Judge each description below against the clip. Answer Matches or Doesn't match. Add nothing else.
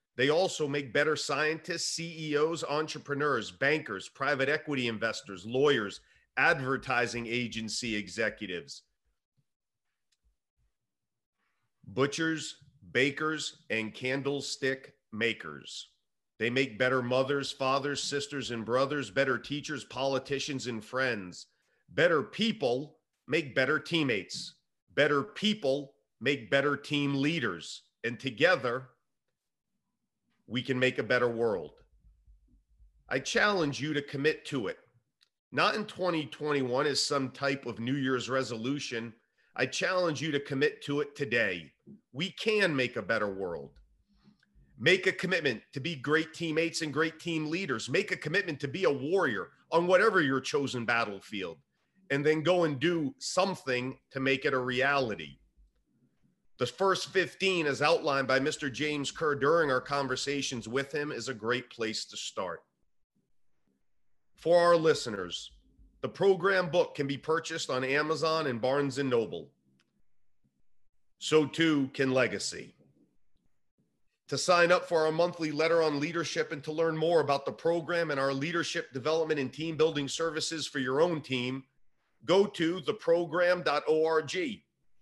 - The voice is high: Doesn't match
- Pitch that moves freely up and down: Doesn't match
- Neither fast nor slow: Doesn't match